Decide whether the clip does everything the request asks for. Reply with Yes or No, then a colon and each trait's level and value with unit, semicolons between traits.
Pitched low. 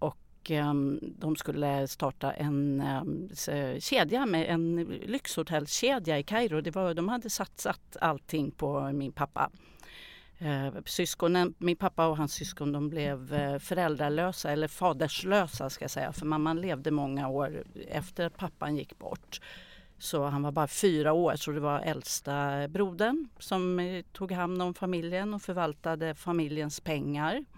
No: medium, 155 Hz